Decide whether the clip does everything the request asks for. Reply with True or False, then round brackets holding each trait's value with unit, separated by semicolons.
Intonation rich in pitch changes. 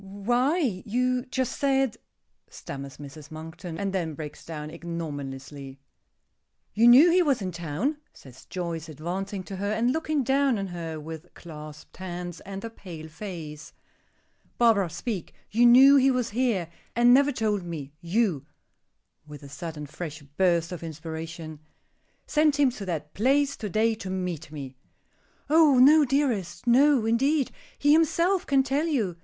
True (7.9 semitones)